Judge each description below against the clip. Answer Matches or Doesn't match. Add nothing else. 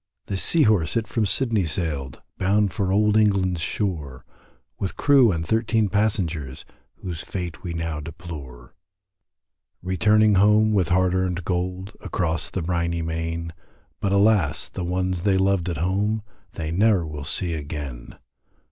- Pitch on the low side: Matches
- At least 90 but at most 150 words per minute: Matches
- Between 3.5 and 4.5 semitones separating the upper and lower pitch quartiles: Matches